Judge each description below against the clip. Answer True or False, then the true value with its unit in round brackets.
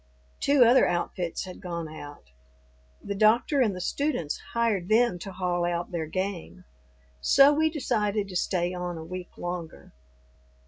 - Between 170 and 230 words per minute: False (150 wpm)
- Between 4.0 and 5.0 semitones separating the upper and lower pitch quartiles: True (4.7 semitones)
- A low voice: False (185 Hz)